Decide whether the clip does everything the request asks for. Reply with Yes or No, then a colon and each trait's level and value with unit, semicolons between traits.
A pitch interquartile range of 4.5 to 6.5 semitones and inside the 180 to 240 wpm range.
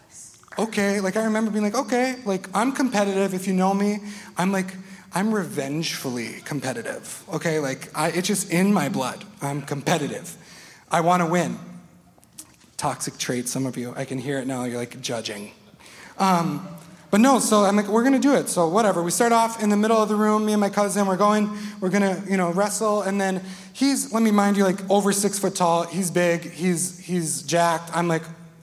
No: average, 3.7 semitones; fast, 205 wpm